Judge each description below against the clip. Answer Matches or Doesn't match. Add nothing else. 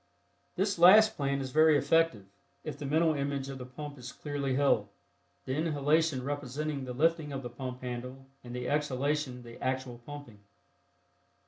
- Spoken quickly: Doesn't match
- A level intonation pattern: Doesn't match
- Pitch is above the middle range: Doesn't match